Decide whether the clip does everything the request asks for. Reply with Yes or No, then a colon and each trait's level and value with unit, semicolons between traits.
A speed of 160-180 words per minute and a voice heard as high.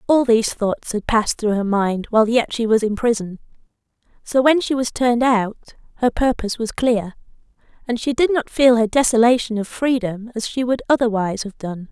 No: average, 195 wpm; high, 230 Hz